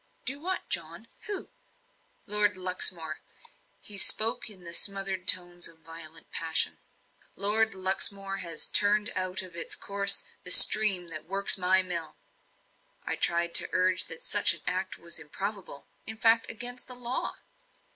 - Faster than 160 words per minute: No, average, 145 wpm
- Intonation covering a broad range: No, average, 3.2 semitones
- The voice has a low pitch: No, high, 190 Hz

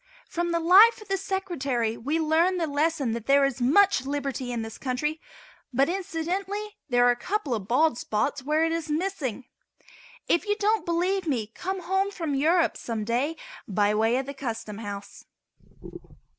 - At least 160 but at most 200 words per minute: Yes, average, 175 wpm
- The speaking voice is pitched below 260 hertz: No, very high, 300 Hz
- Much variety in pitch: Yes, wide, 6.7 semitones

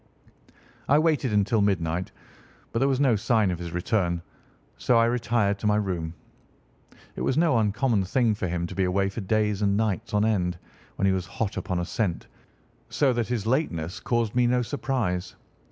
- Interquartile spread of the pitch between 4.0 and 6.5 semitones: Yes, average, 4.3 semitones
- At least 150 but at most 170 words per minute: No, average, 185 wpm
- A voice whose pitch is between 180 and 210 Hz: No, low, 105 Hz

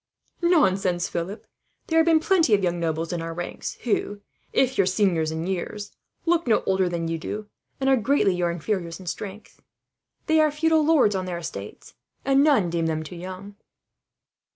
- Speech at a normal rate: Yes, average, 180 wpm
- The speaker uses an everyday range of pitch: No, wide, 7.7 semitones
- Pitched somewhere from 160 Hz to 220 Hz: Yes, high, 190 Hz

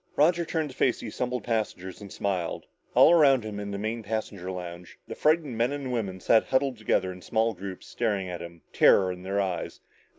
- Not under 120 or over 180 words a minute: No, fast, 205 wpm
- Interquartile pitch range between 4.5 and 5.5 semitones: Yes, average, 5.1 semitones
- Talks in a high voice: No, low, 110 Hz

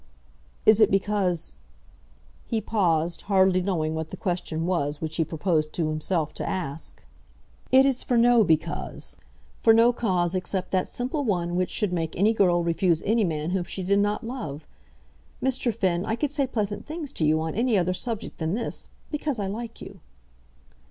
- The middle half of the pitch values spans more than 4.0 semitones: Yes, wide, 5.4 semitones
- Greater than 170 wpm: Yes, average, 180 wpm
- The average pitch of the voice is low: No, medium, 185 Hz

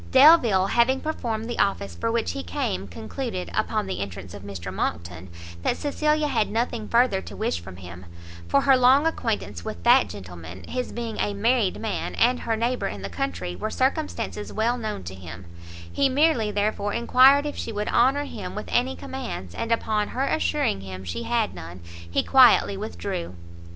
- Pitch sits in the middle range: No, high, 210 Hz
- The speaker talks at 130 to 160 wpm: No, average, 180 wpm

